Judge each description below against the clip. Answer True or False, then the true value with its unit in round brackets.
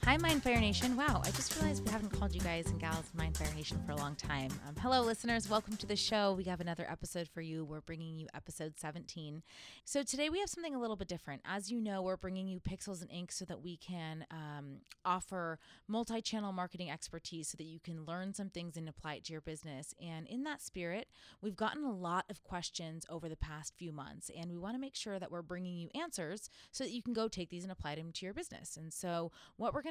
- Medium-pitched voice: True (175 Hz)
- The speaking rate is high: True (250 wpm)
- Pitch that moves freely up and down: False (4.6 semitones)